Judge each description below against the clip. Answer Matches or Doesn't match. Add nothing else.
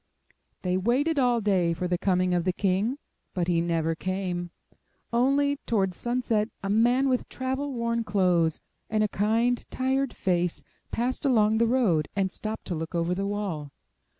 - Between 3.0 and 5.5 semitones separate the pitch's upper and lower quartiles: Matches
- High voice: Matches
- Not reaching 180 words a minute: Matches